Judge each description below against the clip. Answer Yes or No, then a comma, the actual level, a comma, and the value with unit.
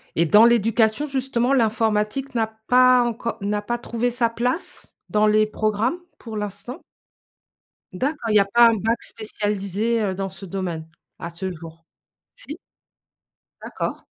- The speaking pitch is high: Yes, high, 220 Hz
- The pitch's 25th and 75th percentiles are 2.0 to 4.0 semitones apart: Yes, average, 3.0 semitones